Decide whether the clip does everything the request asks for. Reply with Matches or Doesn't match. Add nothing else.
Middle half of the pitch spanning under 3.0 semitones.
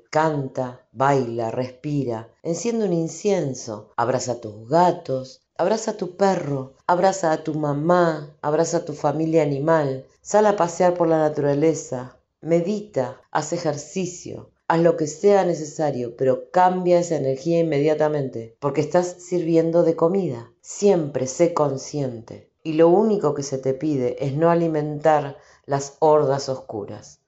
Doesn't match